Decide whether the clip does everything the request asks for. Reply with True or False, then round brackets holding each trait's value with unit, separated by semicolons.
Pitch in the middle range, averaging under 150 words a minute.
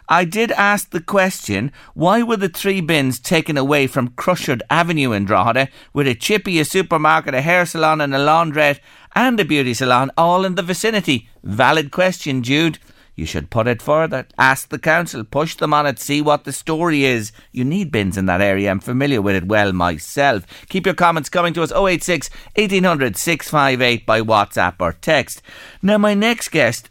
False (150 Hz; 190 wpm)